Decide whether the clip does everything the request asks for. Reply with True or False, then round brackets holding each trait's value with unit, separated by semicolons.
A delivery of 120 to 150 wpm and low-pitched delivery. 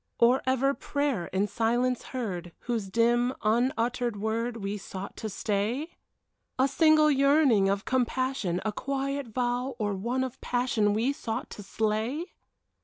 False (140 wpm; 240 Hz)